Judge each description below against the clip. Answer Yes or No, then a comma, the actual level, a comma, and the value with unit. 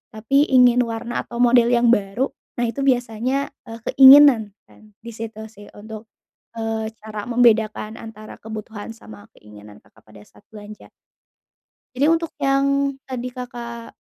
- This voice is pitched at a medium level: No, high, 230 Hz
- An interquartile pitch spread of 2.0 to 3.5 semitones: Yes, average, 2.8 semitones